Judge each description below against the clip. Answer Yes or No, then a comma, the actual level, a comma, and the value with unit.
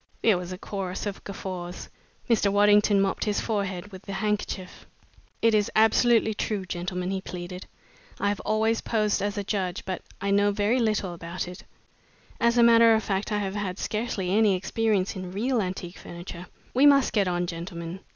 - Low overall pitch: No, high, 200 Hz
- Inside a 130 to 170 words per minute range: No, average, 180 wpm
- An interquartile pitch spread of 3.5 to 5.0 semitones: No, average, 2.8 semitones